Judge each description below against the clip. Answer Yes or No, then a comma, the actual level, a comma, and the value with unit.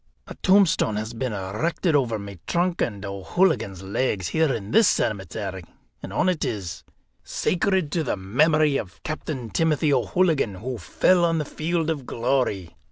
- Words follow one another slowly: No, average, 160 wpm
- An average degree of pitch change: No, wide, 8.1 semitones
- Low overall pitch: Yes, low, 130 Hz